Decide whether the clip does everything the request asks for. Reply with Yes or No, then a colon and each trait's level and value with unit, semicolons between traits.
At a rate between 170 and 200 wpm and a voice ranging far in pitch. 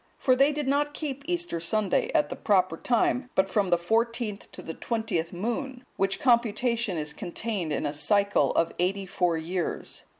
Yes: average, 175 wpm; wide, 5.9 semitones